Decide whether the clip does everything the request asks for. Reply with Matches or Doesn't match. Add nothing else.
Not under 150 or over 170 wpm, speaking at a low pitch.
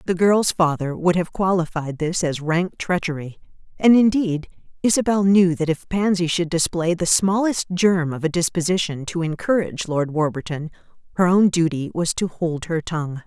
Doesn't match